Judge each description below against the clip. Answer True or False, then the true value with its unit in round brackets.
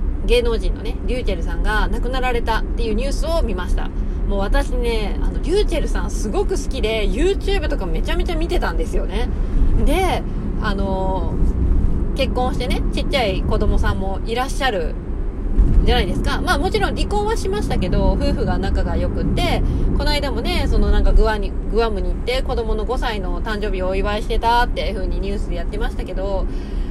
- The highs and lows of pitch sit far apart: False (4.0 semitones)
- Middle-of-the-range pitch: False (230 Hz)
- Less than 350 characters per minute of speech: False (415 characters per minute)